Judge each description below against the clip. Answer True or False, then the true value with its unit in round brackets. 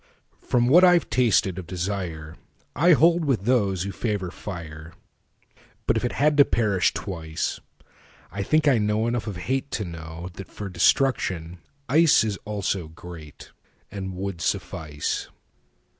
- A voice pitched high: False (100 Hz)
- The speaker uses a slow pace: True (125 wpm)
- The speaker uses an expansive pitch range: True (6.0 semitones)